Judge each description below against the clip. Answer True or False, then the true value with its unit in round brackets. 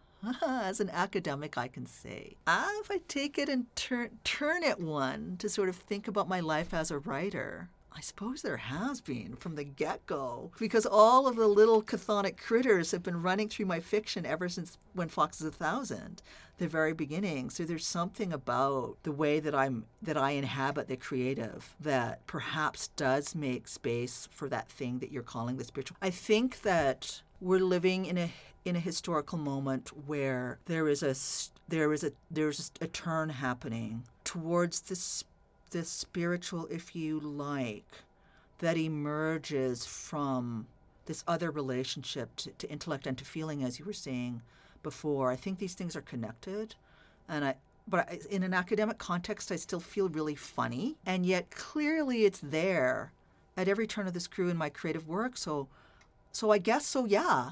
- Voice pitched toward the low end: False (165 Hz)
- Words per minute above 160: True (175 wpm)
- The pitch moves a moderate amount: False (6.2 semitones)